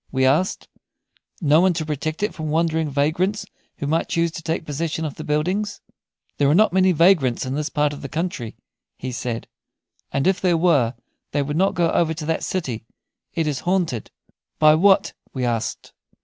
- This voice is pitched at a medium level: Yes, medium, 155 Hz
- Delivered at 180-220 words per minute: Yes, average, 190 wpm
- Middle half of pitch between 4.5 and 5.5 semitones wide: No, average, 3.4 semitones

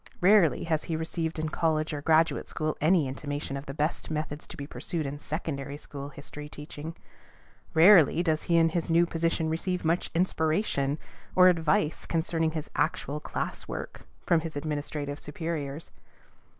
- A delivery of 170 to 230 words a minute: No, average, 160 wpm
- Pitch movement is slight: Yes, narrow, 2.0 semitones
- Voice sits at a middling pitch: Yes, medium, 155 Hz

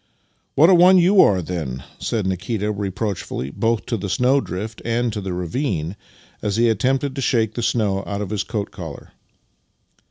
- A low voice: Yes, low, 105 Hz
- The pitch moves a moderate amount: Yes, average, 4.3 semitones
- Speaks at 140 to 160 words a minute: No, average, 190 wpm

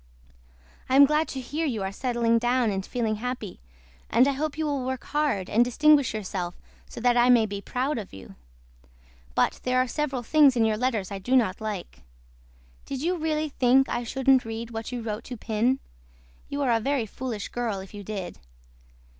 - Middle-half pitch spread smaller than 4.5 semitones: Yes, average, 3.7 semitones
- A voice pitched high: Yes, high, 245 Hz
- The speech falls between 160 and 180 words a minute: No, average, 195 wpm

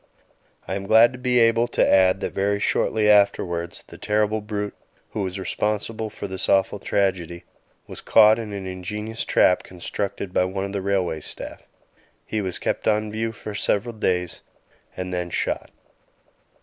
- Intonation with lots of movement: No, narrow, 2.6 semitones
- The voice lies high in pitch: No, low, 100 Hz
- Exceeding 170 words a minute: No, average, 165 wpm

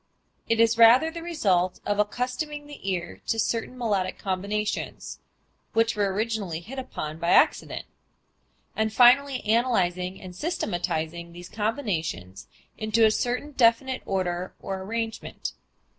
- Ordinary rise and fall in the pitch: Yes, average, 4.9 semitones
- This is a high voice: Yes, high, 215 Hz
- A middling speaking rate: No, slow, 130 wpm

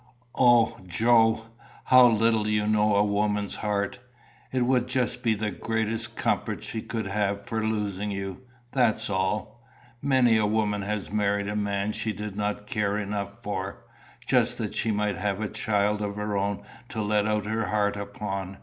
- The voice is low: Yes, low, 105 Hz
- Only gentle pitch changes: Yes, narrow, 1.6 semitones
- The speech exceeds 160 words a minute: Yes, average, 170 wpm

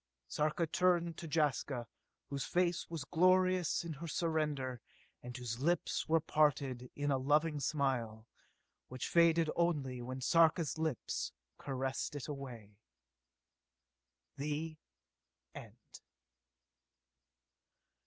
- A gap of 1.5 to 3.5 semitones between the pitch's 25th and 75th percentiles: No, average, 4.2 semitones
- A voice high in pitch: No, medium, 150 Hz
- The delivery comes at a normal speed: No, slow, 105 wpm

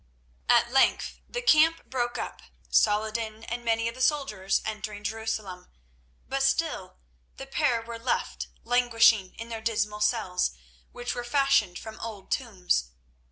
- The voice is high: Yes, high, 230 Hz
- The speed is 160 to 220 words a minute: No, average, 140 wpm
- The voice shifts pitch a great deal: No, average, 3.0 semitones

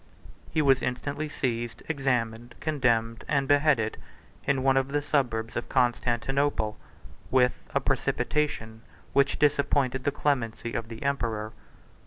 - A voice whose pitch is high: No, low, 130 Hz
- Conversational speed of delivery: No, slow, 125 wpm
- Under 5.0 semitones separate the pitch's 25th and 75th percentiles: Yes, average, 3.6 semitones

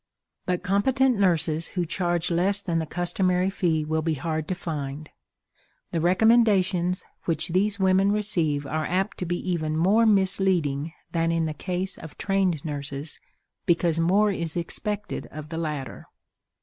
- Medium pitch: Yes, medium, 175 Hz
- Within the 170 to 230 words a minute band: No, average, 150 wpm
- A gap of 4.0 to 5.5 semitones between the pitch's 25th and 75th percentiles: No, average, 3.4 semitones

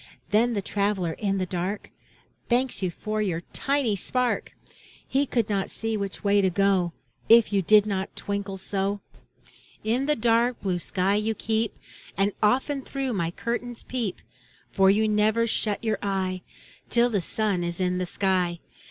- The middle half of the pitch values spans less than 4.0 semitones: Yes, average, 3.0 semitones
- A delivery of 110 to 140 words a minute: No, average, 165 wpm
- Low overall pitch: No, high, 205 Hz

